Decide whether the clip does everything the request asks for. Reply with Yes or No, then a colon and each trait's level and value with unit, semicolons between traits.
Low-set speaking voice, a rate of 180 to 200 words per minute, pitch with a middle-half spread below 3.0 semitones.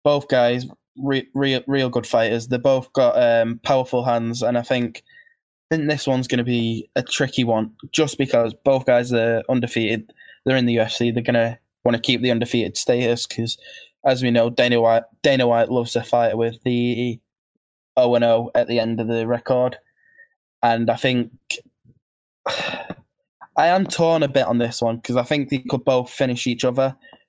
Yes: low, 120 Hz; average, 185 wpm; narrow, 2.4 semitones